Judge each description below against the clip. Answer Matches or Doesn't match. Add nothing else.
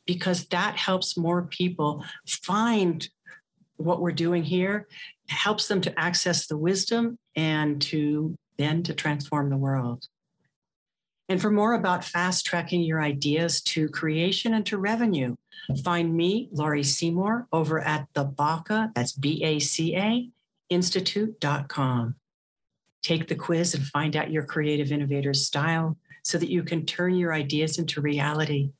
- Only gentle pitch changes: Doesn't match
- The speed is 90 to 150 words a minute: Matches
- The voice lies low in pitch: Doesn't match